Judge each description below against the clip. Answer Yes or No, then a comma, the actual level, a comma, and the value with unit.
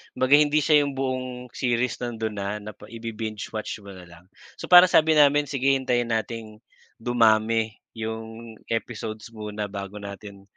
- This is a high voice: No, low, 115 Hz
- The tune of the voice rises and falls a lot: No, average, 3.2 semitones